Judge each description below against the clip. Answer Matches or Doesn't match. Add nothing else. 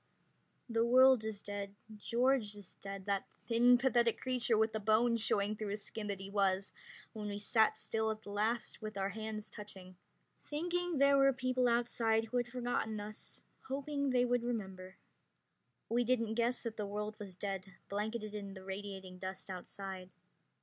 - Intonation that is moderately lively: Matches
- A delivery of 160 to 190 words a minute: Matches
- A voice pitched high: Matches